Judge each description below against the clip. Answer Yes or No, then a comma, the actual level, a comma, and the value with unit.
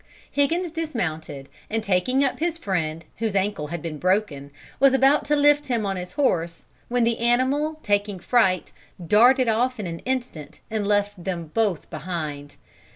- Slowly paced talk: No, average, 160 wpm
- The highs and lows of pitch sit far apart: Yes, wide, 7.0 semitones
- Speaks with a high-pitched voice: Yes, high, 210 Hz